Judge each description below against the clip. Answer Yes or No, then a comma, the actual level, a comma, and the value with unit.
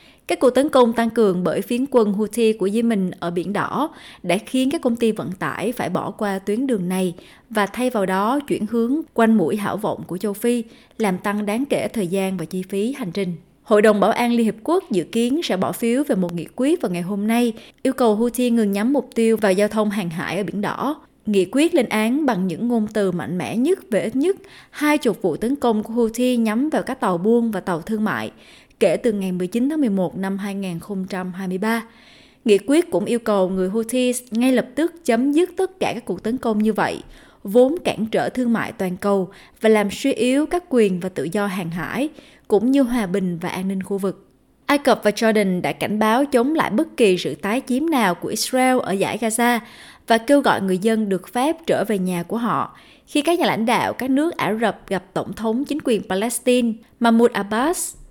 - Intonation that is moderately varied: Yes, average, 4.3 semitones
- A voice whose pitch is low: No, high, 225 Hz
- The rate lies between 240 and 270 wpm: No, average, 230 wpm